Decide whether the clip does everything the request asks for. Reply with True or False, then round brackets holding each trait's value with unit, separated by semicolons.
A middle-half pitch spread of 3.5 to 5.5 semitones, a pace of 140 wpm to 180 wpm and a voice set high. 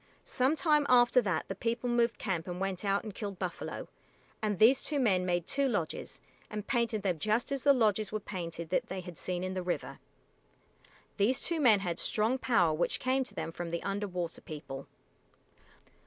False (5.1 semitones; 195 wpm; 205 Hz)